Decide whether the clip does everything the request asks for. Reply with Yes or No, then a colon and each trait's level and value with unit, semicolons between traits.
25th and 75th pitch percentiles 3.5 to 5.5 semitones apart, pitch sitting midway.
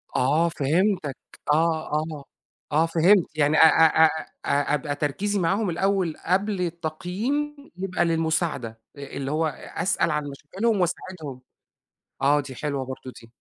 Yes: average, 4.1 semitones; medium, 160 Hz